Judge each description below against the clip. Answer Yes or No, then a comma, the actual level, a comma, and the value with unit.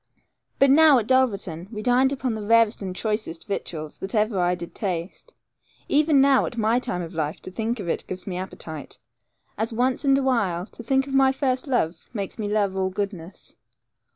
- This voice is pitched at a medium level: No, high, 215 Hz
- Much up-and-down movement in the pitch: Yes, wide, 5.8 semitones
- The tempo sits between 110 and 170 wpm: No, average, 195 wpm